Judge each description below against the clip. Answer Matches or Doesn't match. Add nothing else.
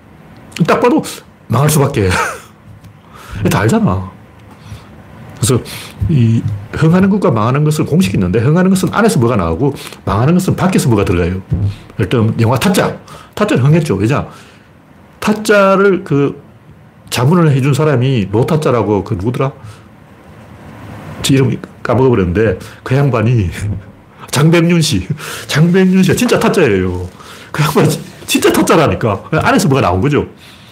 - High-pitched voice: Doesn't match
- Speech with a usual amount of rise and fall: Doesn't match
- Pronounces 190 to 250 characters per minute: Doesn't match